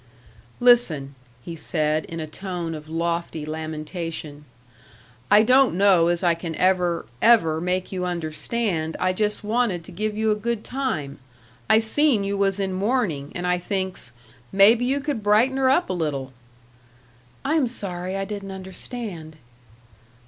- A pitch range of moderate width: Yes, average, 4.9 semitones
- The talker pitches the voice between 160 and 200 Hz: Yes, medium, 185 Hz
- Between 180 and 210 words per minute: No, average, 155 wpm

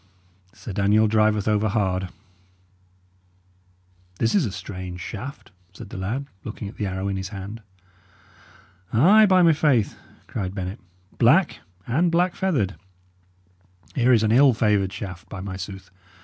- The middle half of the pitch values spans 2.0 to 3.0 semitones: No, average, 4.6 semitones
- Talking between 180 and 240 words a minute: No, average, 145 wpm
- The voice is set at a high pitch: No, low, 105 Hz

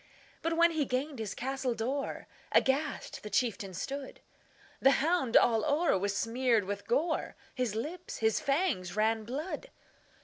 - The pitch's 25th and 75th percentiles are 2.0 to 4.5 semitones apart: No, average, 5.0 semitones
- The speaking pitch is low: No, very high, 255 Hz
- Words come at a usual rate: No, slow, 130 wpm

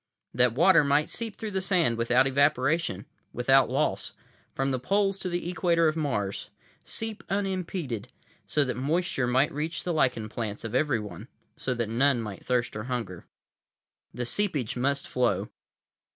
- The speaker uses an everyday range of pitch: No, wide, 5.8 semitones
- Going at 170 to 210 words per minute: No, average, 150 wpm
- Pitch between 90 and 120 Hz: No, low, 135 Hz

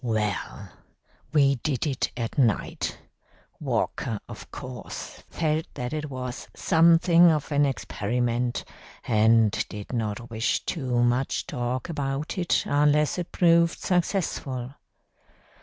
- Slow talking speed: Yes, slow, 115 wpm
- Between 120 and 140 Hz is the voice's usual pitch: Yes, low, 135 Hz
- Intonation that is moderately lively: Yes, average, 4.5 semitones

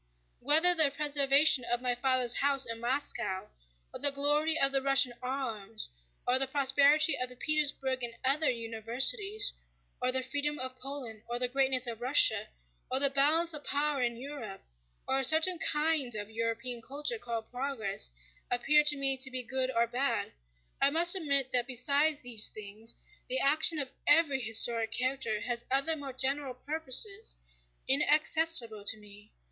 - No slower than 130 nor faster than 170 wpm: Yes, average, 165 wpm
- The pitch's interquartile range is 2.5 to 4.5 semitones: Yes, average, 3.4 semitones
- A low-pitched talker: No, very high, 265 Hz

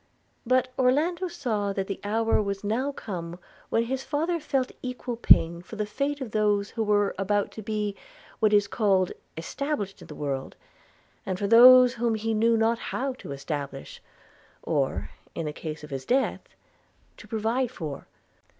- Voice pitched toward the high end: Yes, high, 220 Hz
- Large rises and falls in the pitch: No, average, 4.4 semitones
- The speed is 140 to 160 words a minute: No, average, 170 wpm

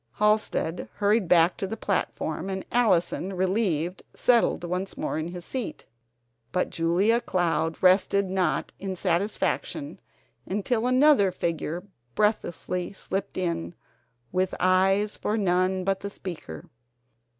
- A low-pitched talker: No, high, 190 Hz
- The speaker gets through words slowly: Yes, slow, 120 wpm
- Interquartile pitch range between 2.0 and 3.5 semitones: Yes, average, 2.8 semitones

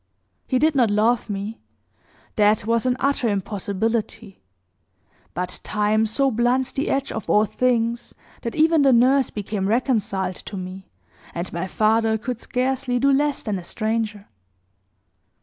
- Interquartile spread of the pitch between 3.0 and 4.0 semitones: Yes, average, 3.5 semitones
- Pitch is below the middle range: No, high, 225 Hz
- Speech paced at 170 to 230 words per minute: No, average, 145 wpm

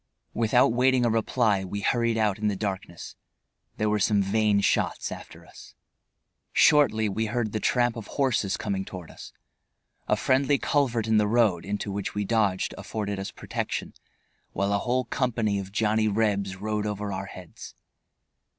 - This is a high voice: No, low, 105 Hz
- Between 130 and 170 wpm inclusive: Yes, average, 165 wpm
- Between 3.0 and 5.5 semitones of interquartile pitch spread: No, narrow, 2.6 semitones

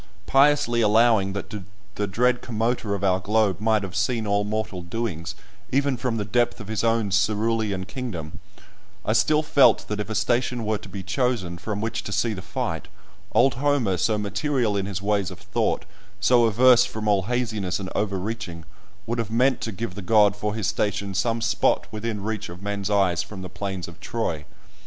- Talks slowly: No, average, 190 wpm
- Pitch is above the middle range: No, low, 105 Hz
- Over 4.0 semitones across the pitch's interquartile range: No, average, 2.9 semitones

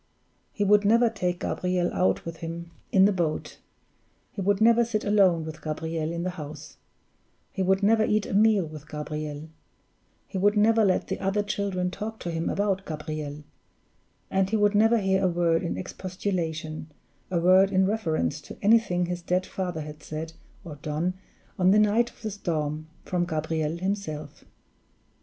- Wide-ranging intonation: No, average, 4.1 semitones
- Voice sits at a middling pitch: Yes, medium, 180 Hz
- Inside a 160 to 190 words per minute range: Yes, average, 170 wpm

